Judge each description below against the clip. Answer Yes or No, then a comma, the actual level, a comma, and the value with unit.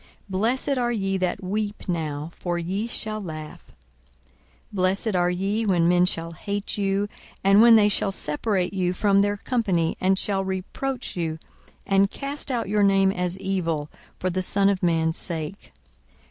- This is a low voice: No, high, 195 Hz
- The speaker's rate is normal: Yes, average, 165 wpm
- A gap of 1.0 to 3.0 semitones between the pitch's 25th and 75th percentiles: Yes, narrow, 2.6 semitones